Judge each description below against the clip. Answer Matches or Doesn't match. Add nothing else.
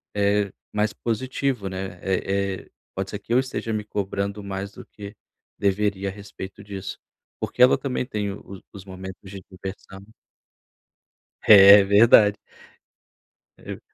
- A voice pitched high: Doesn't match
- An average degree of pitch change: Doesn't match